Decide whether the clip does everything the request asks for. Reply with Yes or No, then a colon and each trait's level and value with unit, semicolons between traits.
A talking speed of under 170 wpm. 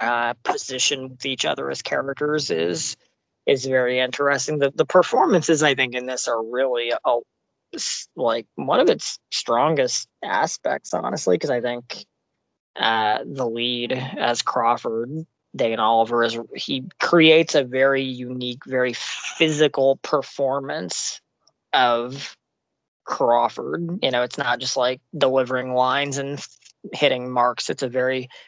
Yes: slow, 135 wpm